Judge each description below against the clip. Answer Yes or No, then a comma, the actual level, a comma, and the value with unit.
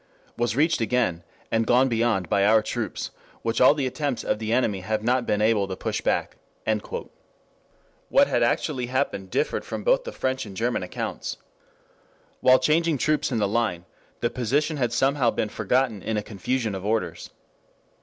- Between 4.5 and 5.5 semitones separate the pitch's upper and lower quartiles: No, average, 3.6 semitones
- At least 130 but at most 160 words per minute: No, average, 175 wpm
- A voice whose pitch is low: Yes, low, 120 Hz